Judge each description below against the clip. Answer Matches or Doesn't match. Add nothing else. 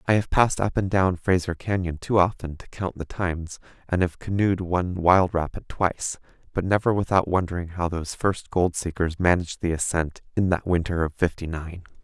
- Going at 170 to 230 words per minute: Matches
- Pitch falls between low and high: Doesn't match